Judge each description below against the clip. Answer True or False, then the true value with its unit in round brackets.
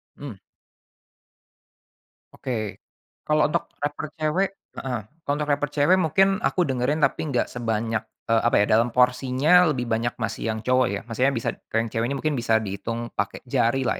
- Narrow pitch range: False (4.2 semitones)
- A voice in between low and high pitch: False (125 Hz)